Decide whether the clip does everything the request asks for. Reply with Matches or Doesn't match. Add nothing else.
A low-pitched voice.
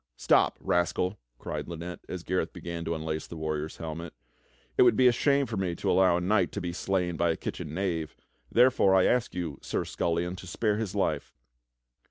Matches